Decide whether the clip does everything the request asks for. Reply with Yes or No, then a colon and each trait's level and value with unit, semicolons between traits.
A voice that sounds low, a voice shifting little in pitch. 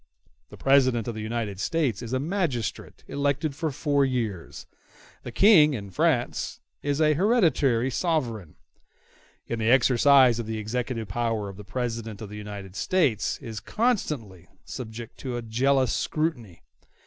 No: low, 120 Hz; average, 4.6 semitones